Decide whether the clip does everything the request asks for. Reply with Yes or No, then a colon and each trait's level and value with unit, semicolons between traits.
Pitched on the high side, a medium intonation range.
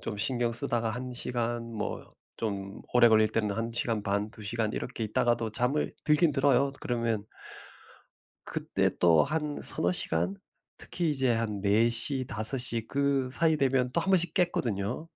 No: low, 120 Hz; average, 3.8 semitones